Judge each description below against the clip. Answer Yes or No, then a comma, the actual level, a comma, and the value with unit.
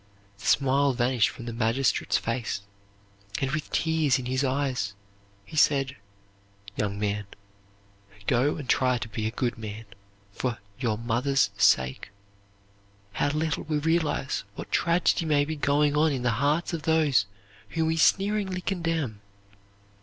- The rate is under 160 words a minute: Yes, average, 145 wpm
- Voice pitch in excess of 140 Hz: No, low, 135 Hz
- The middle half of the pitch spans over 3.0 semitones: Yes, average, 4.9 semitones